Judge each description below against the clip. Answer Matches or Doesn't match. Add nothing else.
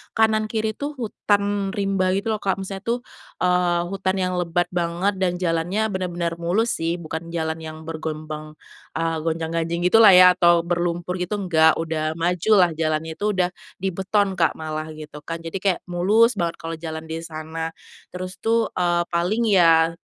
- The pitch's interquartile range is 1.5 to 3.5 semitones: Matches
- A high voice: Doesn't match